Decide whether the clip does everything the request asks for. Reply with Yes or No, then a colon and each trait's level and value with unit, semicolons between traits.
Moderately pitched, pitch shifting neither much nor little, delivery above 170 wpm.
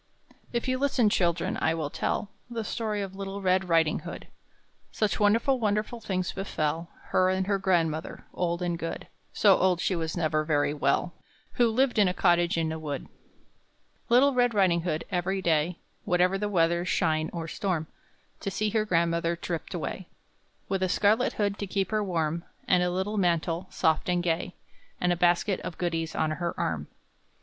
Yes: medium, 180 Hz; average, 3.3 semitones; average, 180 wpm